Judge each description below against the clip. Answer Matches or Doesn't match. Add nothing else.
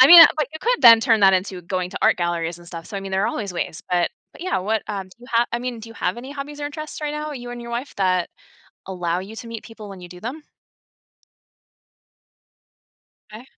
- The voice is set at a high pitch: Matches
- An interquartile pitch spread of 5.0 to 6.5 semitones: Matches